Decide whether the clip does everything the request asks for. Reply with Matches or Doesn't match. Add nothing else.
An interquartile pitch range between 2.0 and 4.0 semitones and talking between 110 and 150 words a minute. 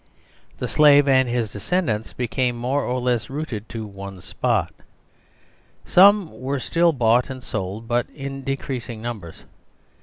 Matches